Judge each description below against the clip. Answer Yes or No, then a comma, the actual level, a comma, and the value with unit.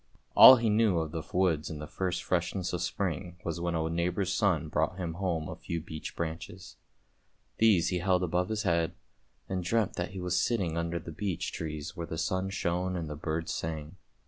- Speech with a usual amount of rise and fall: No, narrow, 2.3 semitones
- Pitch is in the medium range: No, very low, 85 Hz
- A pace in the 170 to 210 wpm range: Yes, average, 200 wpm